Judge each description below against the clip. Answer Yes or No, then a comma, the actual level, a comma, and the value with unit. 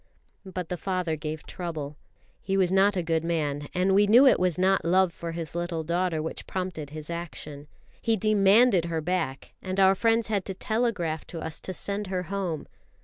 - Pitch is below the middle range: No, medium, 180 Hz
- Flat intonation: No, average, 3.1 semitones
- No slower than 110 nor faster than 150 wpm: No, average, 195 wpm